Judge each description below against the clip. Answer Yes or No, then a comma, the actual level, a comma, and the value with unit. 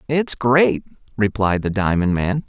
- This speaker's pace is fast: No, average, 145 wpm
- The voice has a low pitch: Yes, low, 115 Hz